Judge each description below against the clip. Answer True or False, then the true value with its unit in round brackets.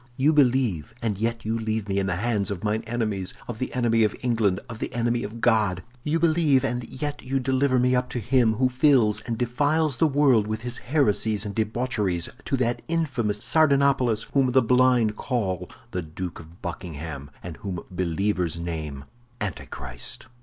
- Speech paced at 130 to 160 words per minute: False (175 wpm)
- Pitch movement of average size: True (4.6 semitones)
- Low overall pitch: True (115 Hz)